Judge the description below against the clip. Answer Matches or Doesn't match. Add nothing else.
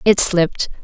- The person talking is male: Doesn't match